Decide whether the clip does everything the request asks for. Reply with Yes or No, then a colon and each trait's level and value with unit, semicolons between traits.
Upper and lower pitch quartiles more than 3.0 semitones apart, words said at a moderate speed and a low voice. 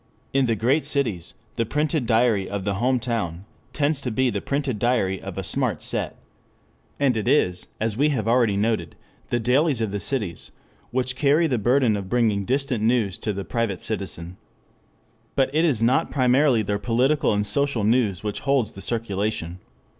Yes: average, 4.5 semitones; average, 180 wpm; low, 115 Hz